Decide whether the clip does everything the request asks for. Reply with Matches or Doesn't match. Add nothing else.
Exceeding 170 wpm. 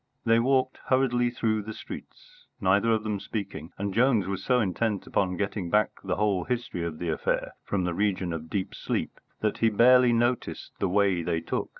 Matches